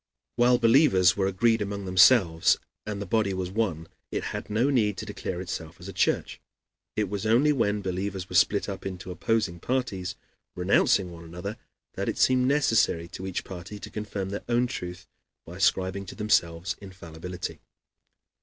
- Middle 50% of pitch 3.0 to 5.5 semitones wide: Yes, average, 3.4 semitones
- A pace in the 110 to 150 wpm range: No, average, 170 wpm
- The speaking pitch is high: No, low, 100 Hz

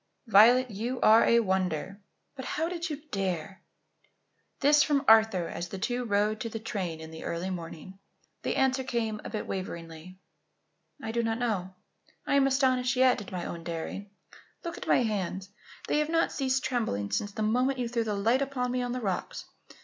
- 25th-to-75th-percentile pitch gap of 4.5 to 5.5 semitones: Yes, average, 5.2 semitones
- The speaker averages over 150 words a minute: Yes, average, 190 wpm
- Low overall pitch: No, high, 220 Hz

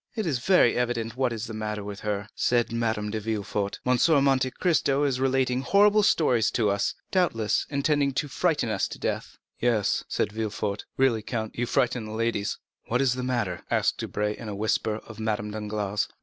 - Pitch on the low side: Yes, low, 115 Hz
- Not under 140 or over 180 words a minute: No, average, 190 wpm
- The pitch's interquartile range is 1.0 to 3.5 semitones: No, average, 3.9 semitones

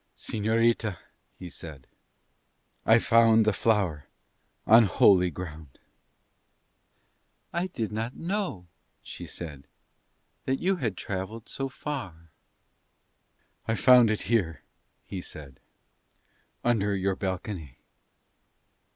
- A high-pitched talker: No, low, 105 Hz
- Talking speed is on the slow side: Yes, slow, 100 wpm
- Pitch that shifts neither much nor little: Yes, average, 4.6 semitones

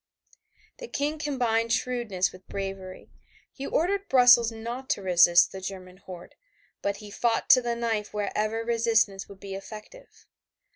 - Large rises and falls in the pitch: No, average, 4.1 semitones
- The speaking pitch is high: Yes, high, 225 Hz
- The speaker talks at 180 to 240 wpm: No, average, 145 wpm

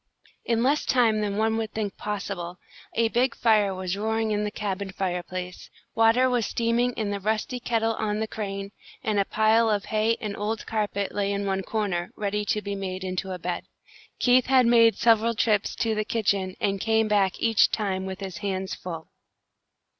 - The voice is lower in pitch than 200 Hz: No, high, 210 Hz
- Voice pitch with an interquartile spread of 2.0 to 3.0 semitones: Yes, narrow, 2.4 semitones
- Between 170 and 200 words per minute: Yes, average, 190 wpm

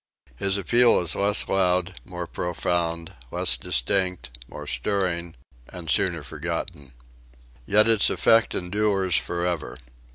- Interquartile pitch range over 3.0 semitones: No, average, 2.7 semitones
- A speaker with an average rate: No, slow, 110 wpm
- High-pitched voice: No, very low, 90 Hz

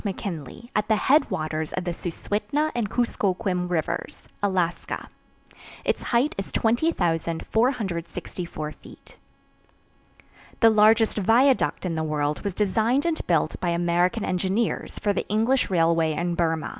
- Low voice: No, high, 190 Hz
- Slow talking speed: Yes, slow, 125 wpm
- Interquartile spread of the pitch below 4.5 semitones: No, average, 5.0 semitones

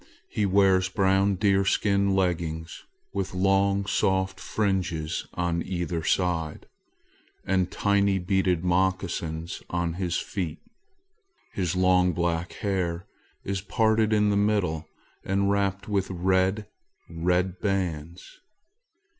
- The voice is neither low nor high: No, very low, 95 Hz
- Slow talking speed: Yes, slow, 105 wpm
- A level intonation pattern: Yes, narrow, 2.1 semitones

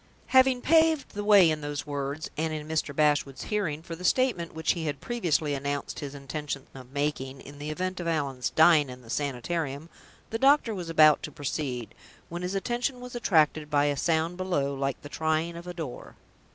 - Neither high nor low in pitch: Yes, medium, 155 Hz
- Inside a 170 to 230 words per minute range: Yes, average, 195 wpm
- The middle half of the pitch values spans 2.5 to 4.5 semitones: Yes, average, 3.9 semitones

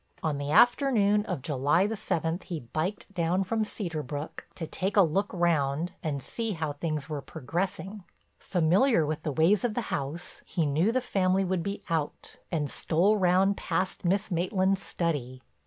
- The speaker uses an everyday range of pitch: Yes, average, 4.2 semitones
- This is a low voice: No, medium, 175 Hz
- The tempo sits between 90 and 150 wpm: No, average, 170 wpm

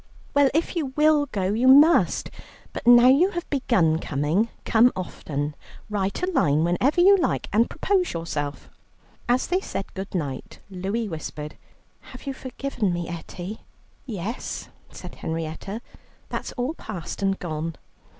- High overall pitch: Yes, high, 210 Hz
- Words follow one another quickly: No, average, 145 wpm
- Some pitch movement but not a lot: No, wide, 8.4 semitones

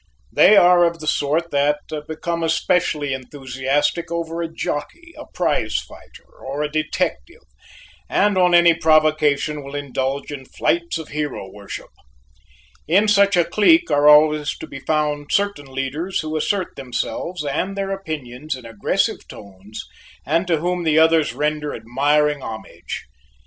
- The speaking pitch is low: No, medium, 155 Hz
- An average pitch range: Yes, average, 3.1 semitones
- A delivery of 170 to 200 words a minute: No, average, 145 wpm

